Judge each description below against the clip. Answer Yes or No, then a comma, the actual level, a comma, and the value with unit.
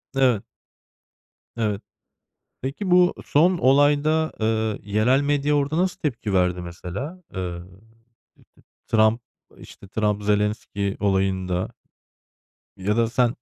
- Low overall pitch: Yes, low, 110 Hz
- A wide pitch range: Yes, wide, 6.4 semitones